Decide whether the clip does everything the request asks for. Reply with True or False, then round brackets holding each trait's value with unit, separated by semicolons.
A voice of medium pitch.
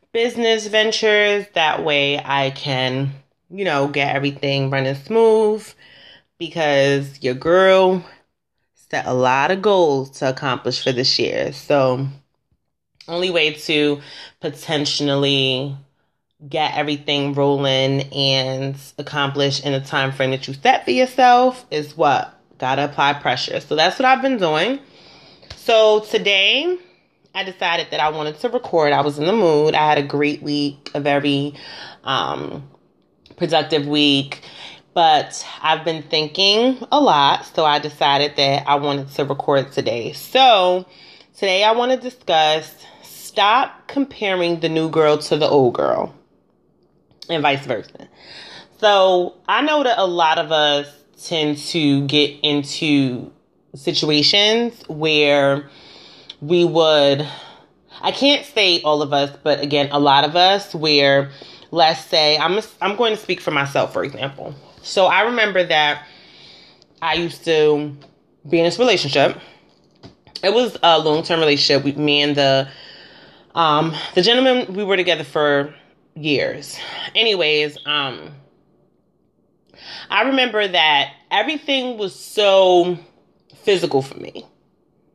True (150 Hz)